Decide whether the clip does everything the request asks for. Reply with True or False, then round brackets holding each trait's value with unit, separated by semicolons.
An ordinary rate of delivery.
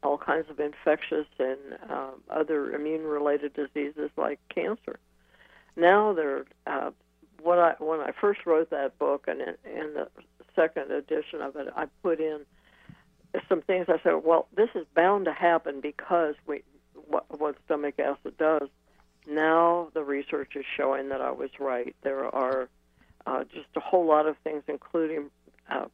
True (160 wpm)